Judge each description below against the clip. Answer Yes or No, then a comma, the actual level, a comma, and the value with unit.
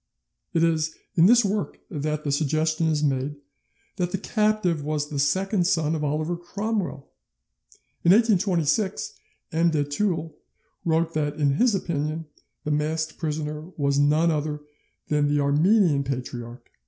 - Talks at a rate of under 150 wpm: Yes, average, 140 wpm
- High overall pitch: No, medium, 155 Hz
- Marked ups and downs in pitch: No, average, 3.0 semitones